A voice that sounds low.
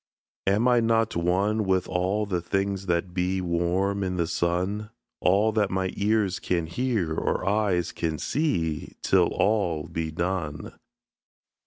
Yes: very low, 95 Hz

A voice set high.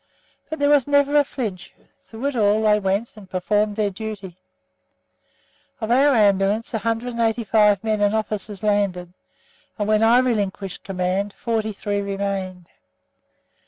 Yes: high, 210 Hz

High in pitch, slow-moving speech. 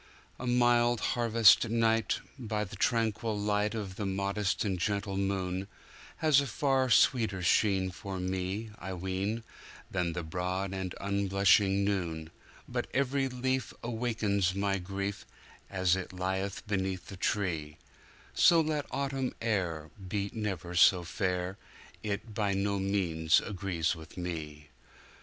No: low, 100 Hz; slow, 115 wpm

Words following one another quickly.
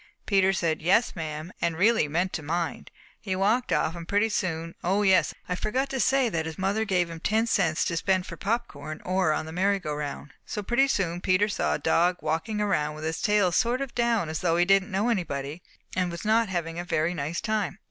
Yes: fast, 225 wpm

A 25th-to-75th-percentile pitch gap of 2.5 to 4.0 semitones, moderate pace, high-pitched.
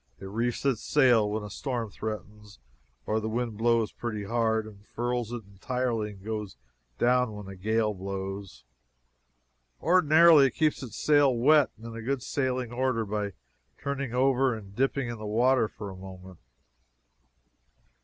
No: average, 3.5 semitones; average, 160 wpm; low, 115 Hz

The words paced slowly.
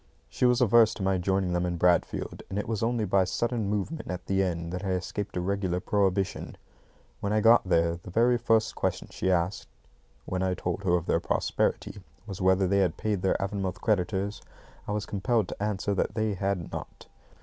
No: fast, 205 wpm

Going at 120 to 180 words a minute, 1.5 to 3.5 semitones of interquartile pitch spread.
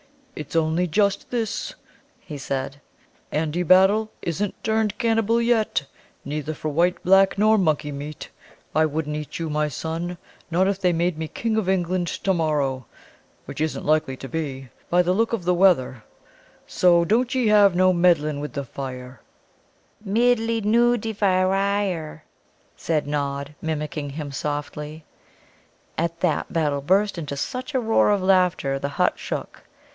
No: average, 150 wpm; average, 5.0 semitones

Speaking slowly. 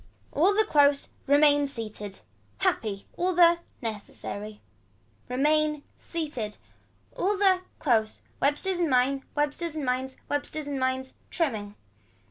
Yes: slow, 115 wpm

